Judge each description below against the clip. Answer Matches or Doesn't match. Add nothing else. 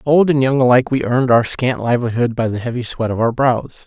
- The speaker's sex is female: Doesn't match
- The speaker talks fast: Matches